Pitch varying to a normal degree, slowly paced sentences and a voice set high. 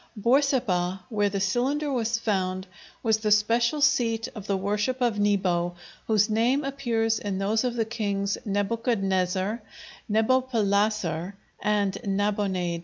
Yes: average, 3.1 semitones; slow, 125 wpm; high, 210 Hz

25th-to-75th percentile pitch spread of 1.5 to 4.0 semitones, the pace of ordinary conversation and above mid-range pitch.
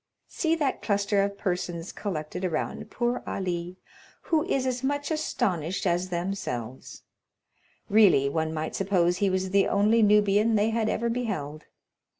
No: average, 4.6 semitones; average, 145 wpm; high, 195 Hz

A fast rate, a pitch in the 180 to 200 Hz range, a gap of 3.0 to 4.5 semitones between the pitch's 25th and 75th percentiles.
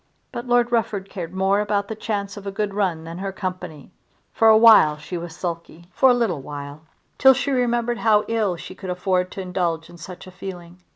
Yes: fast, 215 wpm; high, 190 Hz; average, 3.9 semitones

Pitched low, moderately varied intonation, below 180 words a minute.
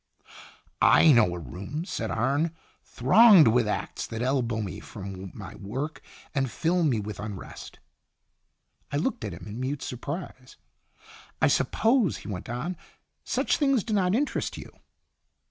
No: low, 130 Hz; wide, 8.0 semitones; average, 160 wpm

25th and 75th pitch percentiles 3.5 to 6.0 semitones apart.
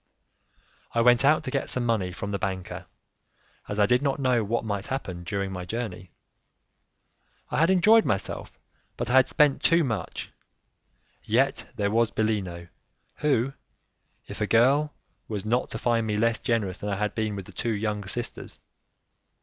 Yes: average, 3.9 semitones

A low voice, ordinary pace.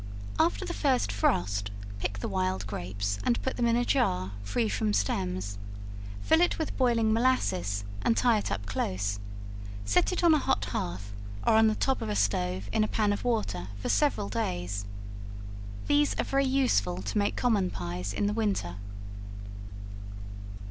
Yes: low, 100 Hz; average, 170 wpm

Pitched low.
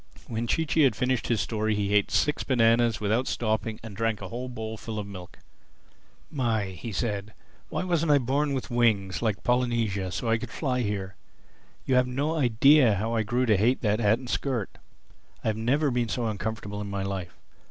Yes: low, 115 Hz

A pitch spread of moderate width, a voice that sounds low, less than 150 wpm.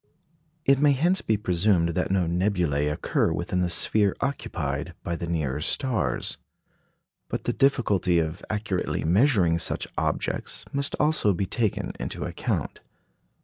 No: wide, 6.0 semitones; very low, 95 Hz; average, 140 wpm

